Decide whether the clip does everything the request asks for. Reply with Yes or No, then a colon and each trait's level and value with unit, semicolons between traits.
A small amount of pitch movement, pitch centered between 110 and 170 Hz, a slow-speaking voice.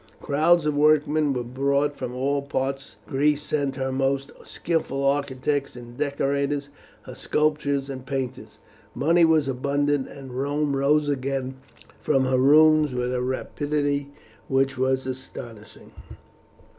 Yes: narrow, 1.8 semitones; medium, 140 Hz; slow, 130 wpm